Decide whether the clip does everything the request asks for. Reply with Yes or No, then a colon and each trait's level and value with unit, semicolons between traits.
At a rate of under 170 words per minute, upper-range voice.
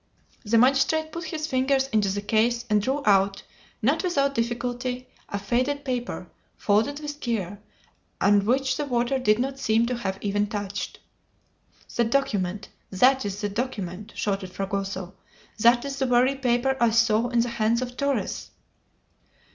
Yes: average, 155 wpm; high, 235 Hz